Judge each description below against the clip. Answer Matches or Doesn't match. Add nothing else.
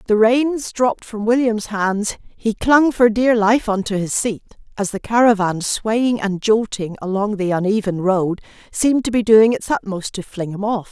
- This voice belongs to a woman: Matches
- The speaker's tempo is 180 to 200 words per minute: Matches